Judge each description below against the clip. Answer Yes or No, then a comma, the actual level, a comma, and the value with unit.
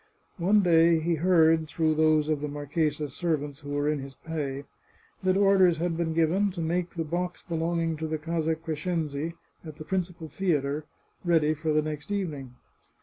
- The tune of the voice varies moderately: No, narrow, 2.2 semitones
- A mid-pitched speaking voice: Yes, medium, 160 Hz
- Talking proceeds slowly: No, average, 185 wpm